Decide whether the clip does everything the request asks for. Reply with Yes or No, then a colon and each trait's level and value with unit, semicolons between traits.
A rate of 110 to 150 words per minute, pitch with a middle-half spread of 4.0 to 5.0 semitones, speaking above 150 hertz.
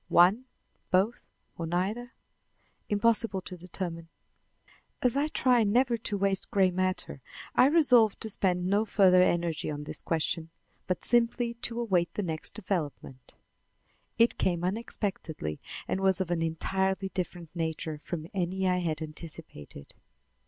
Yes: average, 140 wpm; average, 4.6 semitones; medium, 185 Hz